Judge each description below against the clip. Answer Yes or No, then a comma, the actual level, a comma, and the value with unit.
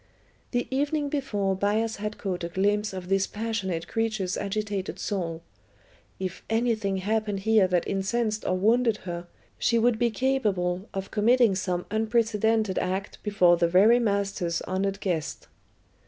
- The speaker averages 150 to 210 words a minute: No, average, 140 wpm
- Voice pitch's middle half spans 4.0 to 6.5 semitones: No, average, 3.1 semitones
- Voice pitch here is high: Yes, high, 205 Hz